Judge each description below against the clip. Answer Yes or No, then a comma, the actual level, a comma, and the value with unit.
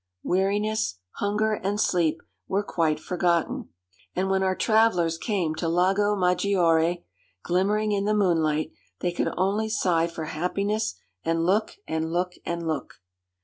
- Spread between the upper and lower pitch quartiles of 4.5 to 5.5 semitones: No, average, 3.5 semitones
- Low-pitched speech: No, medium, 180 Hz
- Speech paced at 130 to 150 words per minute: Yes, average, 140 wpm